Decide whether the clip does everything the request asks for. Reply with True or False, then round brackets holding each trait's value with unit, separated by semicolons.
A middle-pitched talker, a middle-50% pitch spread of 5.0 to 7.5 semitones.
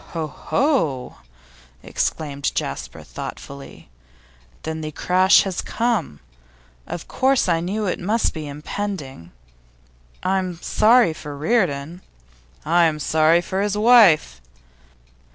True (170 Hz; 5.5 semitones)